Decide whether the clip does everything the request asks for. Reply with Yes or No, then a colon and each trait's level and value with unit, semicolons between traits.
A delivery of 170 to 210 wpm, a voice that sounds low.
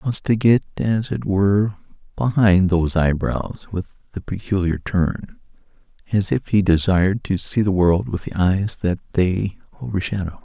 No: average, 160 wpm; very low, 95 Hz